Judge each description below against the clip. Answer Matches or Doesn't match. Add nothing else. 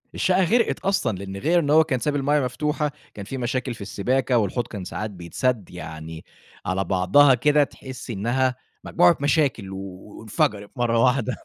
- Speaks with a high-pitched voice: Doesn't match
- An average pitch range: Doesn't match